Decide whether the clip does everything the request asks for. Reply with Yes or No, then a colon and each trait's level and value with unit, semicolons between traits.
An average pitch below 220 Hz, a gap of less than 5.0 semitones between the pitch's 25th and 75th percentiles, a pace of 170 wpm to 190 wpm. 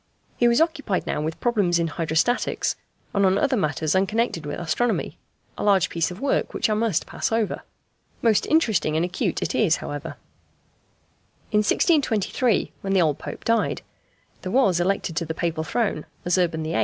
No: high, 190 Hz; wide, 5.6 semitones; average, 175 wpm